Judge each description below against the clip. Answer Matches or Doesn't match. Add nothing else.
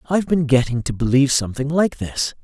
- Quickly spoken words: Doesn't match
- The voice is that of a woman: Doesn't match